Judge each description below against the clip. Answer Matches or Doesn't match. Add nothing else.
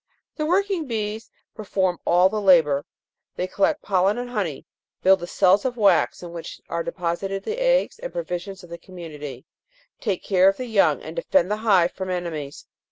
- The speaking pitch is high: Matches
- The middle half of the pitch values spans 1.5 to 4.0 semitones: Doesn't match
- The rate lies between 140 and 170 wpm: Doesn't match